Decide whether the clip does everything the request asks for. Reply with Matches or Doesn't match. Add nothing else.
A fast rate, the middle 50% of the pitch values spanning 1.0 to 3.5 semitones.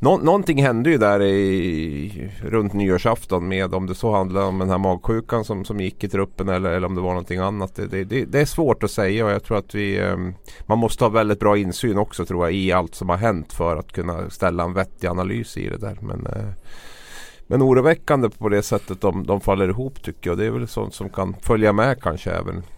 Matches